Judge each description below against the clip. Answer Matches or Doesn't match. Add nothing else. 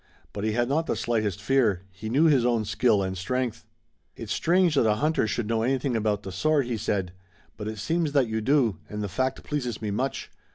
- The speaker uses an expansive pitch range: Doesn't match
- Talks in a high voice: Doesn't match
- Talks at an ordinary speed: Doesn't match